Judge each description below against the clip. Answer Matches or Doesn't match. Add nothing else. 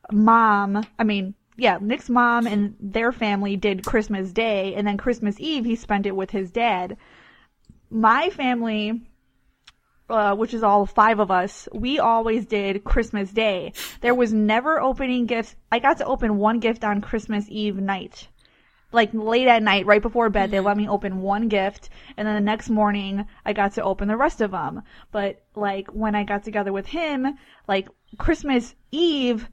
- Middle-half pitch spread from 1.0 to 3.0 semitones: Matches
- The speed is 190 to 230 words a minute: Doesn't match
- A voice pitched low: Doesn't match